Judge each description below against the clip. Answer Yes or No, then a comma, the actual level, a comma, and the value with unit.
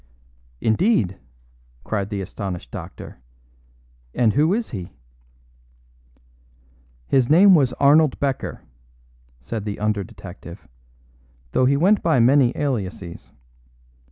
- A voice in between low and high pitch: No, low, 120 Hz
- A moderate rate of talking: No, slow, 100 wpm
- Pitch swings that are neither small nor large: No, wide, 6.7 semitones